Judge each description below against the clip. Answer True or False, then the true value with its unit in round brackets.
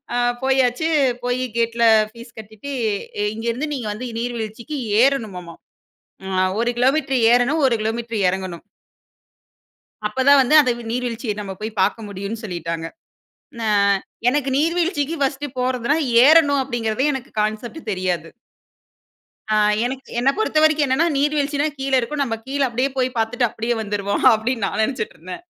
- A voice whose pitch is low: False (245 Hz)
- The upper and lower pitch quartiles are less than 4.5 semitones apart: True (4.0 semitones)